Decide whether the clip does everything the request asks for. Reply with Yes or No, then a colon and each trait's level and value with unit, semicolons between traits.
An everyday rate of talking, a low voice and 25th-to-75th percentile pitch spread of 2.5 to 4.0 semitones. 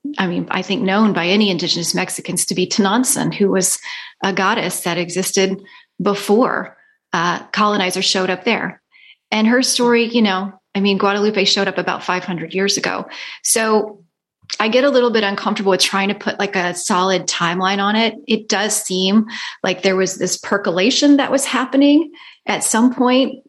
No: average, 175 wpm; high, 200 Hz; average, 3.4 semitones